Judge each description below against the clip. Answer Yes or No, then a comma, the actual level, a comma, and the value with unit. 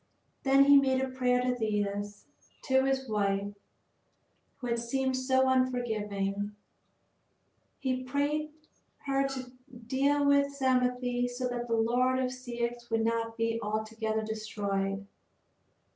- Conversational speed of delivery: No, slow, 125 wpm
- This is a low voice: No, high, 245 Hz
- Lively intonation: No, average, 3.1 semitones